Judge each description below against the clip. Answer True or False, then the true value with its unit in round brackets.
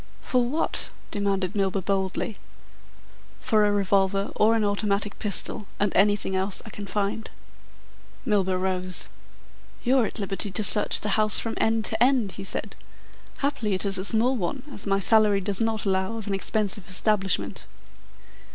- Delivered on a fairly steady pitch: True (2.1 semitones)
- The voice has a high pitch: True (205 Hz)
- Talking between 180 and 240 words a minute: False (160 wpm)